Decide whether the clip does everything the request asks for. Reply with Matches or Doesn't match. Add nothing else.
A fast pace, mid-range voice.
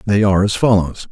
Doesn't match